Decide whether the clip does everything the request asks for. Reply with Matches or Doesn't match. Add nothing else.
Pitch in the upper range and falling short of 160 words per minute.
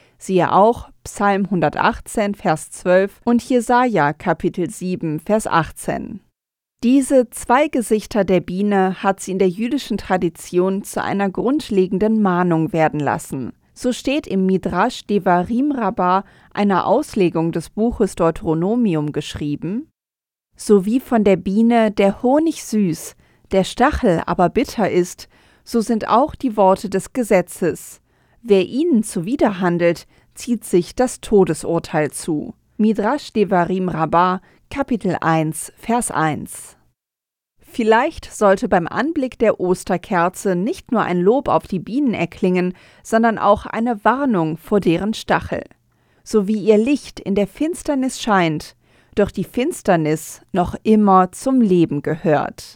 Matches